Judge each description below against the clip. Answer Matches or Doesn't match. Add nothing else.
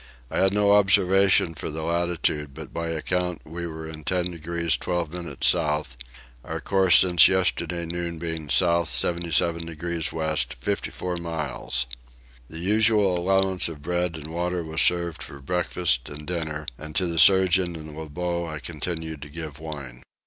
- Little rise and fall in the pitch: Matches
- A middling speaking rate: Matches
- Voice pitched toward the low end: Matches